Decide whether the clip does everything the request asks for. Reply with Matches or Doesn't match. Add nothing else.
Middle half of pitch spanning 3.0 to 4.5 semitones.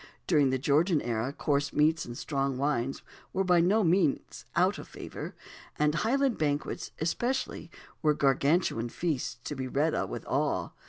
Matches